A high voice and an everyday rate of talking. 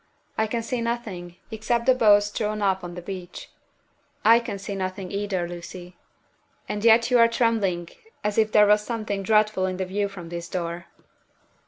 Yes: high, 205 Hz; average, 180 wpm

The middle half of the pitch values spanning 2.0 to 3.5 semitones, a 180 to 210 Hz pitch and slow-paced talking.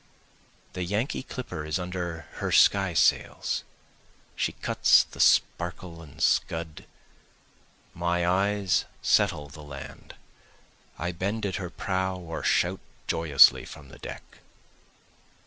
No: narrow, 2.5 semitones; very low, 90 Hz; slow, 115 wpm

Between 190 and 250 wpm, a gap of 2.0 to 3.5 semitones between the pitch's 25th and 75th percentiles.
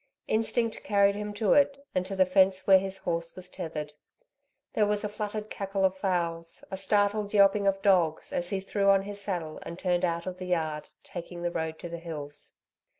Yes: fast, 205 wpm; average, 3.0 semitones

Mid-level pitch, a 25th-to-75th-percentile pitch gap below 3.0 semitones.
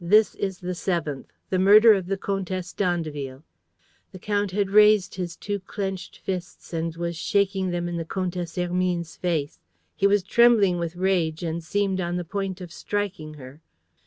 Yes: medium, 180 Hz; narrow, 2.5 semitones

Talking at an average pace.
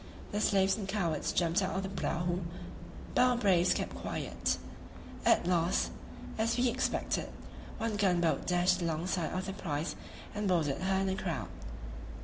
Yes: average, 160 wpm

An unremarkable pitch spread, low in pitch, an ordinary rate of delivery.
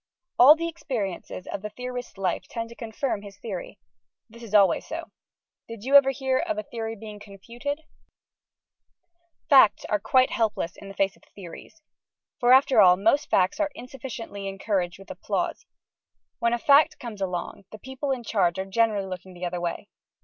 No: average, 5.0 semitones; high, 225 Hz; average, 175 wpm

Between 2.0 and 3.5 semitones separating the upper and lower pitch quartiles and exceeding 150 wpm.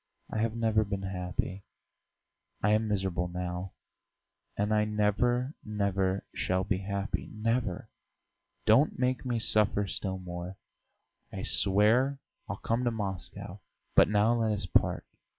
No: average, 2.8 semitones; slow, 135 wpm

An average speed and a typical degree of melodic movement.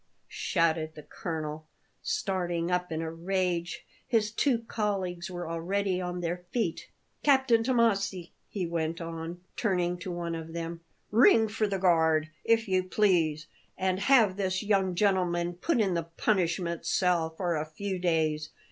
Yes: average, 150 wpm; average, 3.1 semitones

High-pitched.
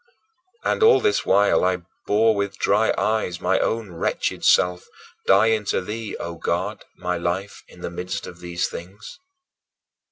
No: very low, 95 Hz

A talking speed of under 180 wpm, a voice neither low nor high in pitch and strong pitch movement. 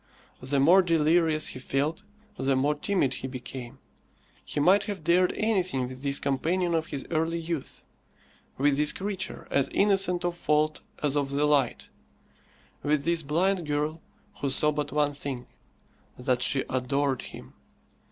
No: average, 150 wpm; medium, 150 Hz; average, 3.8 semitones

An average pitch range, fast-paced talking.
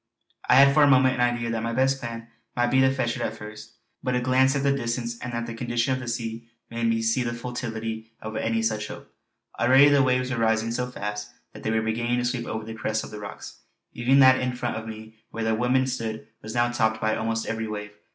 No: narrow, 2.2 semitones; fast, 250 wpm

